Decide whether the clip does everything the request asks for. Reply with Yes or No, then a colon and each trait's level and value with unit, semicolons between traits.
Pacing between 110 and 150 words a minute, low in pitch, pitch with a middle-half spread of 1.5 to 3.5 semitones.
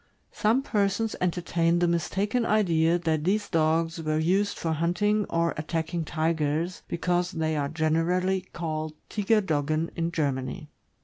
No: slow, 135 wpm; medium, 170 Hz; average, 2.8 semitones